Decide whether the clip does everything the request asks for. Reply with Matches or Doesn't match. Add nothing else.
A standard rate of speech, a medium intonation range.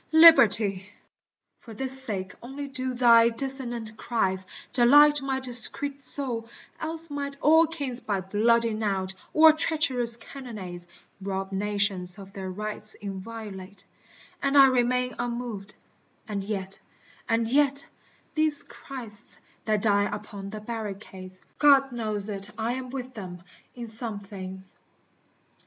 Doesn't match